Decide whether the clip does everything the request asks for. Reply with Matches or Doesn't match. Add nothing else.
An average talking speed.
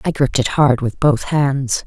Doesn't match